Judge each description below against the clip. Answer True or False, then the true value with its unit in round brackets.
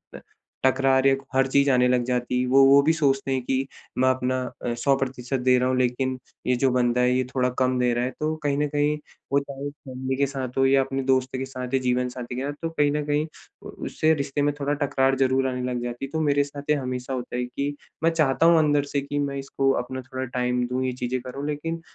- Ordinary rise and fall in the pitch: False (1.9 semitones)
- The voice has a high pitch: False (135 Hz)